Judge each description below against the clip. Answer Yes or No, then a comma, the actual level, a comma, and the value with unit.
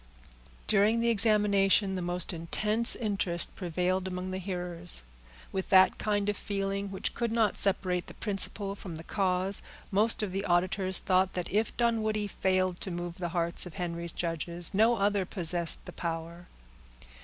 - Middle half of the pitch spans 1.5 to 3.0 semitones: Yes, narrow, 2.6 semitones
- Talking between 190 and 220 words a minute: No, average, 160 wpm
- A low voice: No, high, 190 Hz